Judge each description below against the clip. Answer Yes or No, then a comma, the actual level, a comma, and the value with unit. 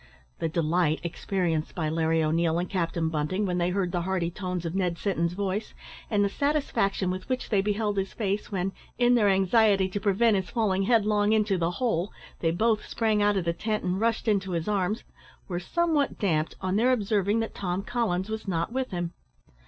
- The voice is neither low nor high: No, high, 195 Hz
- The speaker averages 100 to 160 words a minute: No, average, 200 wpm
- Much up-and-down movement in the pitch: No, average, 3.5 semitones